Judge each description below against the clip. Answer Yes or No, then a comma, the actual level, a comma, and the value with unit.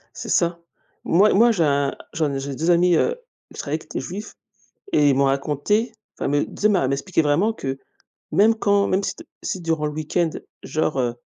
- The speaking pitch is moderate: Yes, medium, 160 Hz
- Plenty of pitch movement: Yes, wide, 5.8 semitones